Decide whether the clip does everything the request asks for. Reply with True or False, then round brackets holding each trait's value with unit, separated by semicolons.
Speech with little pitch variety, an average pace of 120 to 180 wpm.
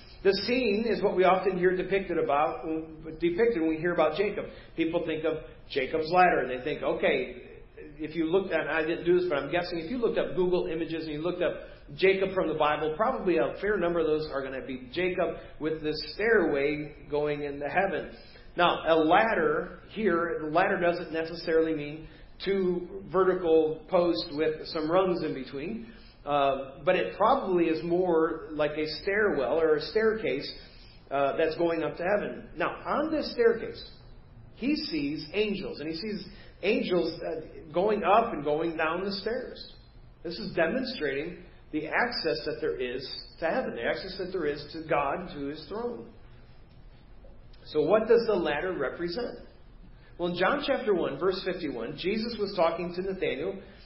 False (3.8 semitones; 175 wpm)